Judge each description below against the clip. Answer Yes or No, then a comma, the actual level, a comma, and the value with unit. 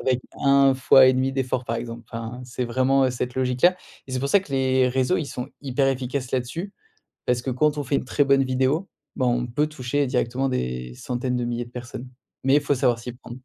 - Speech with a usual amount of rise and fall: No, narrow, 1.8 semitones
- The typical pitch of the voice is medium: No, low, 130 Hz